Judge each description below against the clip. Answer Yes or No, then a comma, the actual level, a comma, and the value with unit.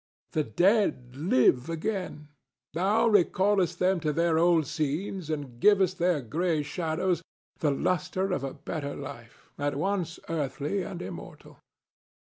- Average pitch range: Yes, average, 4.3 semitones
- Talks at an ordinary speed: No, slow, 130 wpm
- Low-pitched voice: No, medium, 165 Hz